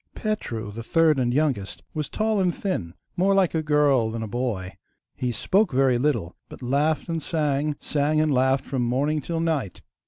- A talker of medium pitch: Yes, medium, 145 Hz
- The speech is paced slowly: No, average, 185 wpm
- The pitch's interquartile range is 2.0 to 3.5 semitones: No, average, 4.7 semitones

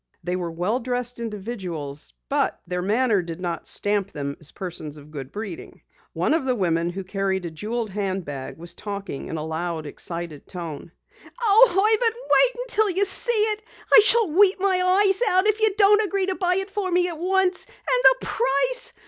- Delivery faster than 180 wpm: Yes, average, 190 wpm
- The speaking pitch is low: No, high, 230 Hz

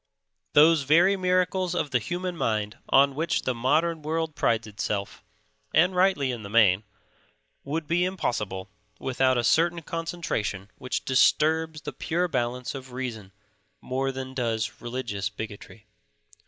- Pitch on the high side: No, low, 135 Hz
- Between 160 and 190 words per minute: No, average, 140 wpm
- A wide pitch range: Yes, wide, 6.4 semitones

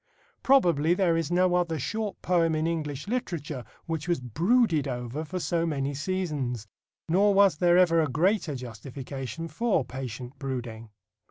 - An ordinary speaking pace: Yes, average, 150 wpm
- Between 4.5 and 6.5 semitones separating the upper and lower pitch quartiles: Yes, average, 5.1 semitones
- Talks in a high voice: No, medium, 160 Hz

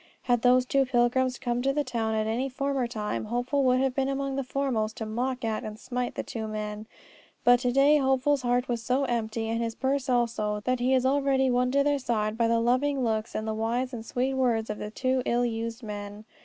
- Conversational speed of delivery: No, fast, 230 wpm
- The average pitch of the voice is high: Yes, high, 245 Hz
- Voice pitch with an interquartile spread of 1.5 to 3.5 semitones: Yes, average, 2.8 semitones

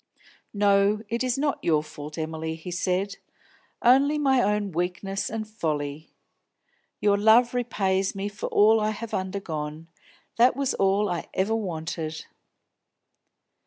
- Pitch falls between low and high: No, high, 200 Hz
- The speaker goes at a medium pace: No, slow, 130 wpm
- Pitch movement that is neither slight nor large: Yes, average, 5.0 semitones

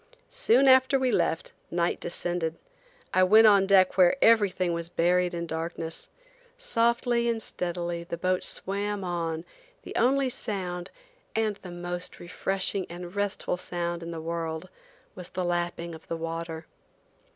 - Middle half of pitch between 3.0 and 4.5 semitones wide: Yes, average, 4.1 semitones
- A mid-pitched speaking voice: Yes, medium, 180 Hz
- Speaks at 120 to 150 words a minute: Yes, average, 140 wpm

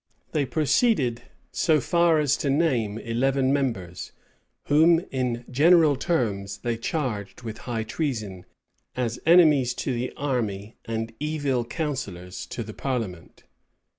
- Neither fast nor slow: No, slow, 125 wpm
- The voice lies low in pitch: Yes, low, 125 Hz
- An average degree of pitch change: Yes, average, 4.9 semitones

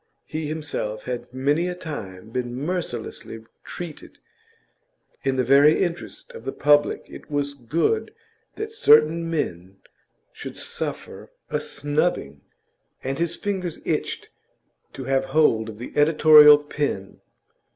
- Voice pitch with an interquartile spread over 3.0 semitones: Yes, average, 4.7 semitones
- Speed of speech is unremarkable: No, slow, 125 wpm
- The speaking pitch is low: No, medium, 145 Hz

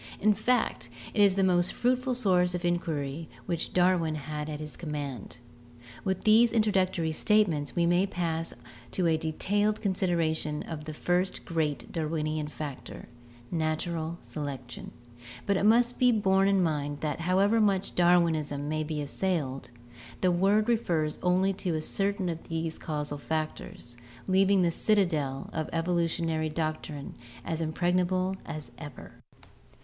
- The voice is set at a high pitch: No, medium, 170 Hz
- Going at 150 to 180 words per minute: No, average, 140 wpm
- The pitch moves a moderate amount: Yes, average, 3.7 semitones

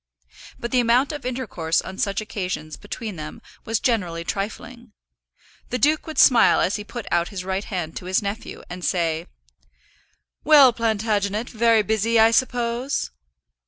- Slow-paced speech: No, average, 155 wpm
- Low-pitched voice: No, high, 220 Hz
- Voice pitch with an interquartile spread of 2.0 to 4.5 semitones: Yes, average, 4.2 semitones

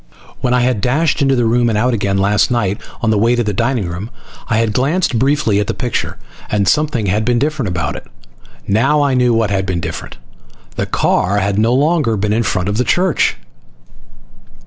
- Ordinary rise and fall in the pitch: Yes, average, 4.1 semitones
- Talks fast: Yes, fast, 210 wpm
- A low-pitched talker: Yes, low, 115 Hz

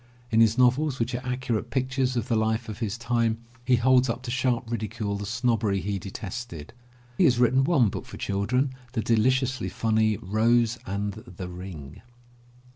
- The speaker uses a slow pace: No, average, 175 wpm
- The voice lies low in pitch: Yes, low, 115 Hz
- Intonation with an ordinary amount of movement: Yes, average, 3.2 semitones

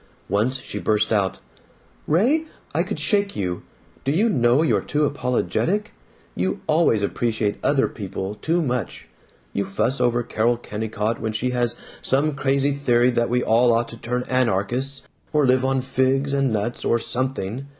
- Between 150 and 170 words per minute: Yes, average, 160 wpm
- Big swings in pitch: No, average, 3.7 semitones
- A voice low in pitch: Yes, low, 125 Hz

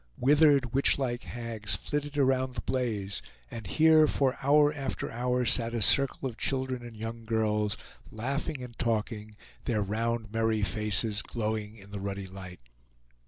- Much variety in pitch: No, average, 3.7 semitones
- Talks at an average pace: Yes, average, 150 wpm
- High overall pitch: No, low, 115 Hz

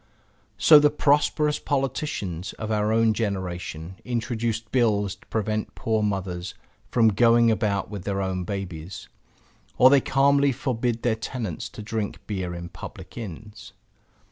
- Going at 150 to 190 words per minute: No, average, 140 wpm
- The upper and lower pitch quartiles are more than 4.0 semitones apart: No, average, 3.7 semitones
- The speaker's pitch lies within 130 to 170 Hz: No, low, 110 Hz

